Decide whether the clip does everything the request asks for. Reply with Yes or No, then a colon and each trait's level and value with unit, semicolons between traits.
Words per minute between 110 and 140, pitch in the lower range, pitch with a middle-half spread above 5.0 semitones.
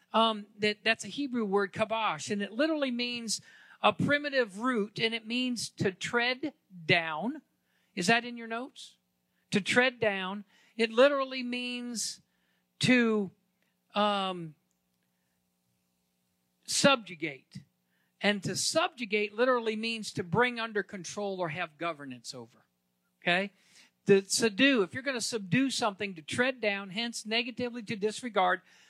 No: slow, 135 wpm; high, 210 Hz; wide, 5.4 semitones